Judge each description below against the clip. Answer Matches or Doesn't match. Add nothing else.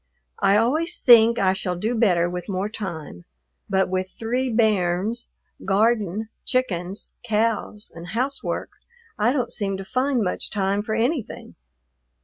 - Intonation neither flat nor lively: Matches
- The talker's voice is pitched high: Matches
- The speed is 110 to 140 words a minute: Matches